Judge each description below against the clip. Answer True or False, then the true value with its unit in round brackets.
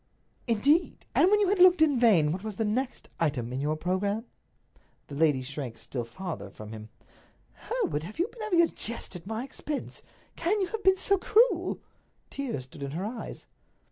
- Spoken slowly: False (190 wpm)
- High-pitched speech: True (220 Hz)